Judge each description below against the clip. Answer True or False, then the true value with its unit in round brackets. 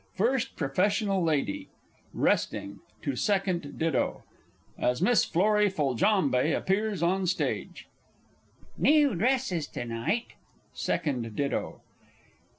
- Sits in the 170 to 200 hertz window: True (185 Hz)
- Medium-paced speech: False (95 wpm)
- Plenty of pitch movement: True (6.6 semitones)